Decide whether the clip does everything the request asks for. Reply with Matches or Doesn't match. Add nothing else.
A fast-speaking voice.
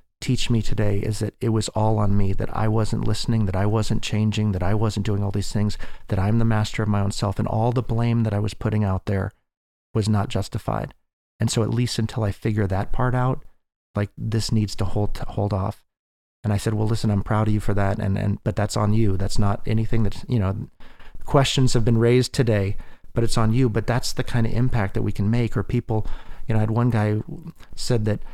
Matches